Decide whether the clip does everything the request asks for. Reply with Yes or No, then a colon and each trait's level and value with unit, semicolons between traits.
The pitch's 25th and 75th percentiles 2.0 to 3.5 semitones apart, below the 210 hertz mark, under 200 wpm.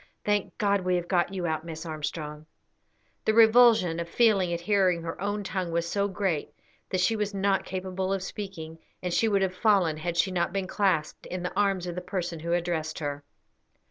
No: average, 2.8 semitones; medium, 185 Hz; fast, 205 wpm